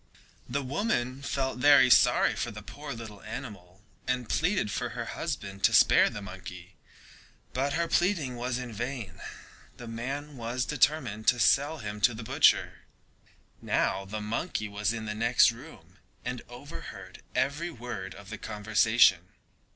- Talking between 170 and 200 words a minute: No, average, 155 wpm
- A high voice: No, low, 120 Hz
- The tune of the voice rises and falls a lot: No, average, 4.6 semitones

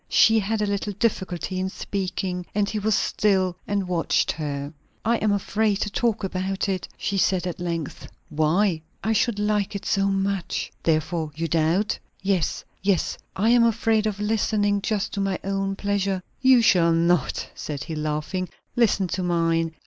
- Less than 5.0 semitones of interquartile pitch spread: Yes, average, 3.2 semitones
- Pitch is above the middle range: Yes, high, 195 Hz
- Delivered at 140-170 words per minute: Yes, average, 165 wpm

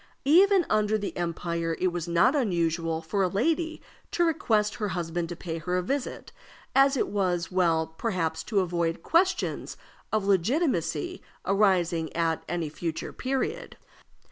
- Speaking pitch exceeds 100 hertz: Yes, medium, 185 Hz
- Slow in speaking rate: No, average, 145 wpm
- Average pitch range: No, wide, 6.6 semitones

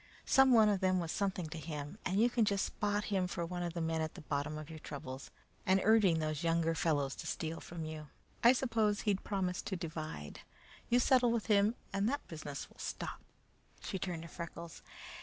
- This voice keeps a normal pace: No, fast, 210 wpm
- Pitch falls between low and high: Yes, medium, 175 Hz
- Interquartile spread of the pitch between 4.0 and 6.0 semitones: Yes, average, 4.6 semitones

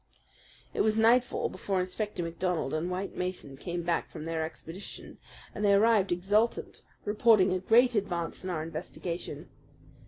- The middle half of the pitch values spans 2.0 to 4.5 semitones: Yes, average, 3.6 semitones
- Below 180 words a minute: Yes, average, 150 wpm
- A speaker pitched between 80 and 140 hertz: No, medium, 185 Hz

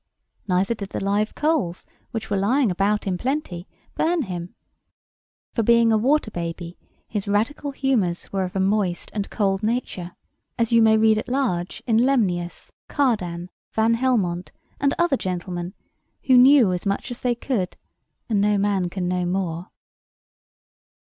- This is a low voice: No, high, 205 Hz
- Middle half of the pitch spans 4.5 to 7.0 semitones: Yes, average, 4.9 semitones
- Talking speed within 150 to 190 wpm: Yes, average, 155 wpm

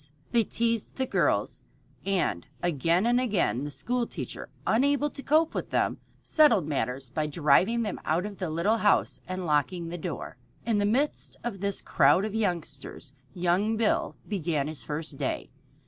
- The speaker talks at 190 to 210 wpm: No, average, 165 wpm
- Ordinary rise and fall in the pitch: No, wide, 6.6 semitones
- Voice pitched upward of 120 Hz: Yes, high, 190 Hz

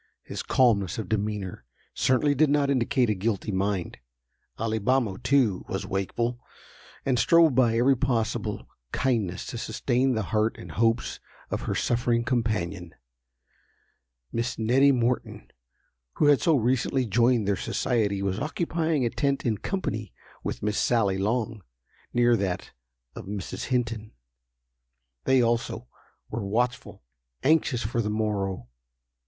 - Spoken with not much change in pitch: No, average, 3.6 semitones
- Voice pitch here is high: No, low, 115 Hz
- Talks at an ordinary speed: No, slow, 130 wpm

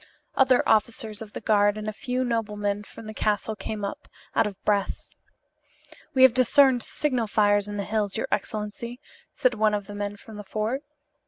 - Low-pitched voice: No, high, 215 Hz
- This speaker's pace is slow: No, average, 185 wpm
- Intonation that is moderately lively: No, narrow, 2.3 semitones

